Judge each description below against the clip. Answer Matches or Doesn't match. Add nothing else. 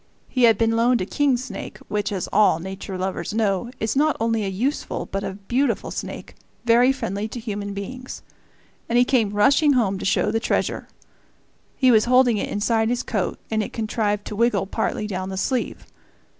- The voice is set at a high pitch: Matches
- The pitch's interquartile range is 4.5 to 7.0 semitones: Doesn't match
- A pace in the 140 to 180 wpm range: Doesn't match